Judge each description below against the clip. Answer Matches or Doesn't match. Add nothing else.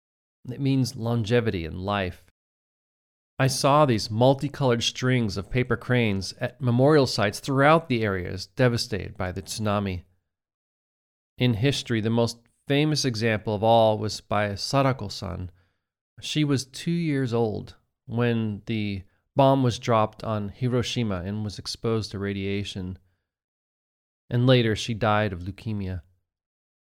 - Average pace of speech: Doesn't match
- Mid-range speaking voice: Doesn't match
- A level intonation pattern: Doesn't match